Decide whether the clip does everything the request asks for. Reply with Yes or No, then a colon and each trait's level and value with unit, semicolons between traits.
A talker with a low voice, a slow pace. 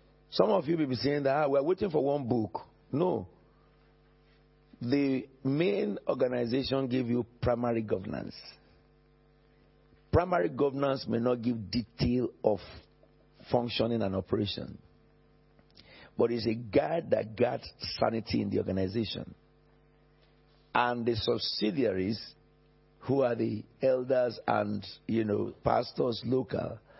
Yes: low, 120 Hz; slow, 120 wpm